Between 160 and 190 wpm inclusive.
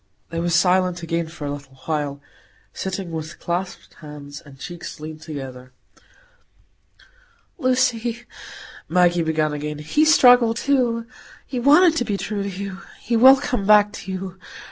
No: average, 145 wpm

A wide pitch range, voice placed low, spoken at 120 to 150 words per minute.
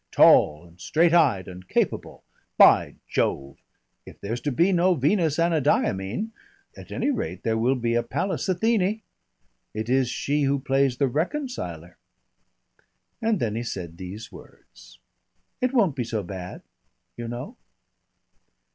Yes: wide, 8.9 semitones; low, 130 Hz; average, 140 wpm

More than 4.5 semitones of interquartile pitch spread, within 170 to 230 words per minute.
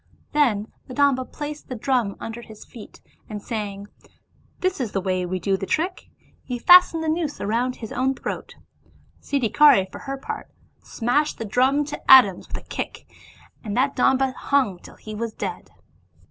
Yes: average, 5.1 semitones; average, 175 wpm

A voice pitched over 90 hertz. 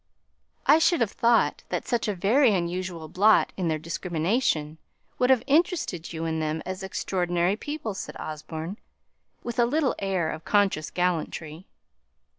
Yes: medium, 185 Hz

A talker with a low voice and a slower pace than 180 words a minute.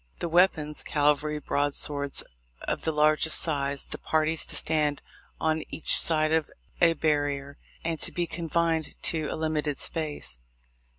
No: medium, 155 Hz; average, 140 wpm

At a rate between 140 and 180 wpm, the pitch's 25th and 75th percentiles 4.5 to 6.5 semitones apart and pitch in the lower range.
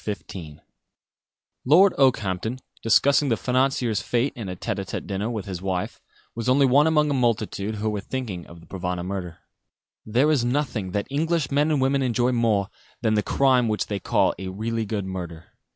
No: average, 190 wpm; average, 5.2 semitones; low, 115 Hz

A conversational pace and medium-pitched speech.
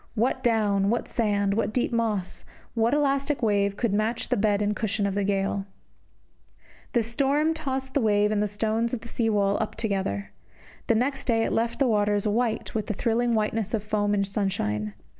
No: average, 195 wpm; high, 215 Hz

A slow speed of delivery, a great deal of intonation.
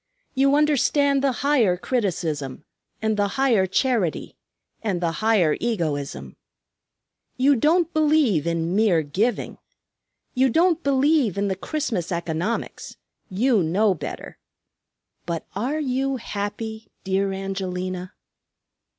Yes: slow, 110 wpm; wide, 6.9 semitones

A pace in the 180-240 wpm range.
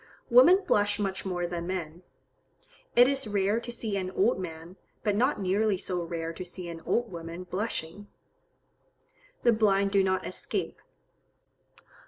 No: average, 150 wpm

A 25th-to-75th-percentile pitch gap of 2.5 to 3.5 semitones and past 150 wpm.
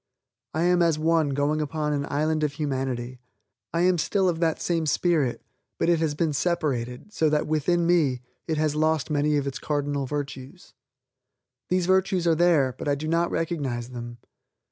Yes: average, 3.0 semitones; average, 180 wpm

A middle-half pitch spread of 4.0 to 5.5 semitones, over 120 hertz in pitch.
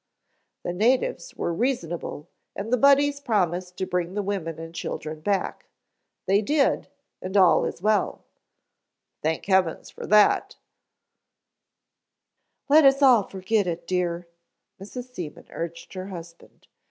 Yes: average, 5.2 semitones; high, 190 Hz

